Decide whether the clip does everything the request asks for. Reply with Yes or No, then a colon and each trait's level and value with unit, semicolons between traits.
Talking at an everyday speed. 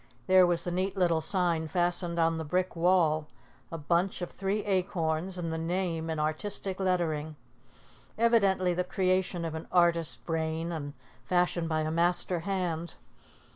Yes: average, 155 wpm